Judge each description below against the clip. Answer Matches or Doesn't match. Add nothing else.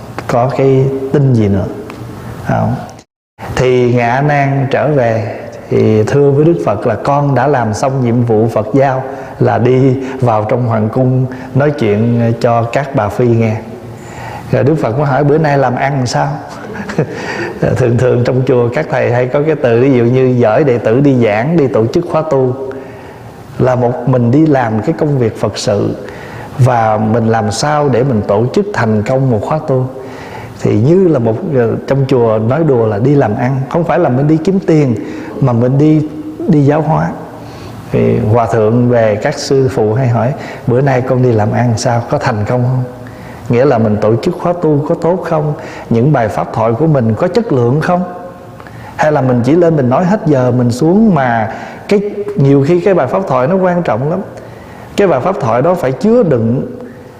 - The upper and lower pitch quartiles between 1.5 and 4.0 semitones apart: Matches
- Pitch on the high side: Doesn't match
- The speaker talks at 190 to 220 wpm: Matches